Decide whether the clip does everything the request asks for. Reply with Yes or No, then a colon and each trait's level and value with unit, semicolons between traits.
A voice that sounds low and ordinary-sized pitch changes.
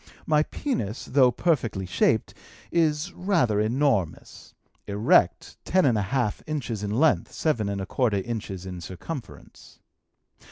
No: low, 120 Hz; wide, 7.0 semitones